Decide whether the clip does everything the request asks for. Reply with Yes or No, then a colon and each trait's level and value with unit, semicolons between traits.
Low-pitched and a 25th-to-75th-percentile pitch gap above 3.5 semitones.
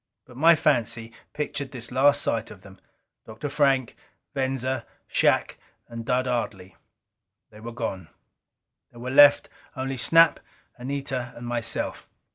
No: low, 125 Hz; average, 3.1 semitones